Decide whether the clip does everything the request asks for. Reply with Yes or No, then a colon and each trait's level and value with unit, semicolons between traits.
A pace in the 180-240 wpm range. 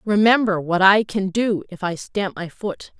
Yes: average, 200 wpm